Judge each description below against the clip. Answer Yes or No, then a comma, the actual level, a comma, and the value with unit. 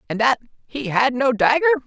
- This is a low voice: No, high, 230 Hz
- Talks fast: No, average, 195 wpm